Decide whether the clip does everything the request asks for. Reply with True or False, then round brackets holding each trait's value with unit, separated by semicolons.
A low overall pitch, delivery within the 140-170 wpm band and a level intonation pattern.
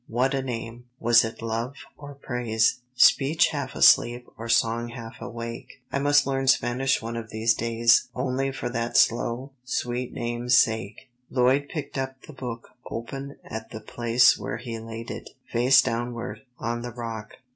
True (120 Hz; 165 wpm; 2.3 semitones)